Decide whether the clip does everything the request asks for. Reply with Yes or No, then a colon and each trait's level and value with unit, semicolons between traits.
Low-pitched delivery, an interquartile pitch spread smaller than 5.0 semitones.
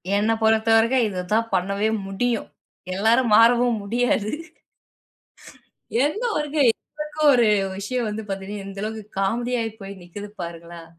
No: high, 220 Hz; average, 3.3 semitones